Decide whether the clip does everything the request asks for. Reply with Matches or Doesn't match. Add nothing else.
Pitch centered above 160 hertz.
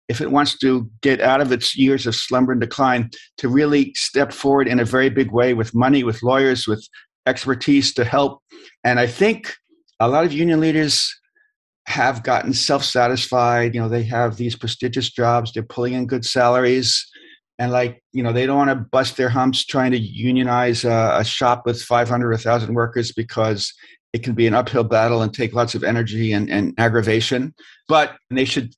Doesn't match